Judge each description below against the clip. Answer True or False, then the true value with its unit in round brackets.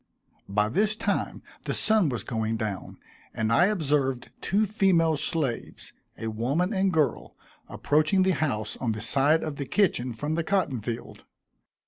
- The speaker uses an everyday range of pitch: False (8.1 semitones)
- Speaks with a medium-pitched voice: True (150 Hz)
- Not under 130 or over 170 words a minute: True (155 wpm)